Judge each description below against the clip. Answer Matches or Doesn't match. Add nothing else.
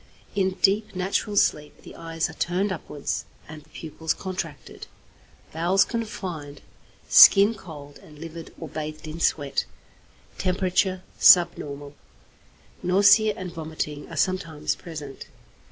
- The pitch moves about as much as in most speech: Matches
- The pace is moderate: Doesn't match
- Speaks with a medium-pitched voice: Matches